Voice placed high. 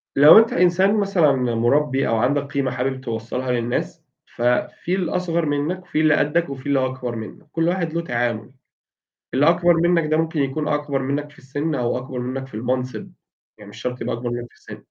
No: medium, 140 Hz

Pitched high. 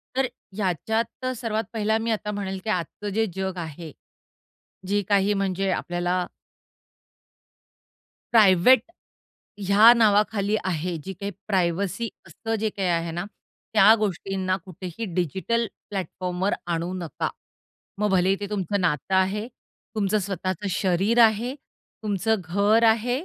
Yes: high, 200 Hz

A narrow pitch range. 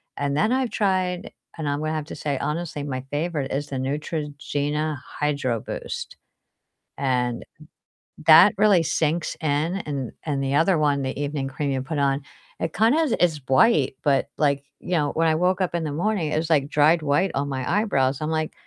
No: average, 3.0 semitones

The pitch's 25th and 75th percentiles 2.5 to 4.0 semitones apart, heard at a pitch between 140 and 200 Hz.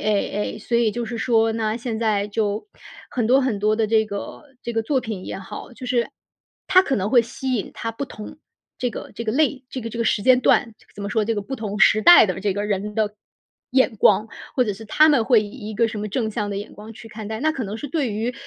No: average, 2.9 semitones; high, 225 Hz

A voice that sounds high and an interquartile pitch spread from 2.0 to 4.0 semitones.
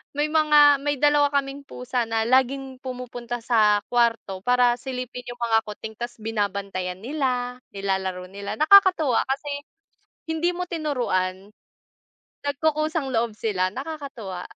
No: very high, 250 Hz; average, 5.0 semitones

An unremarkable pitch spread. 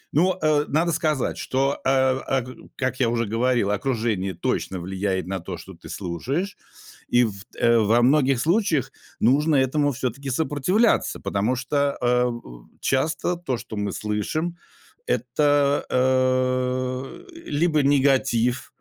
Yes: average, 3.7 semitones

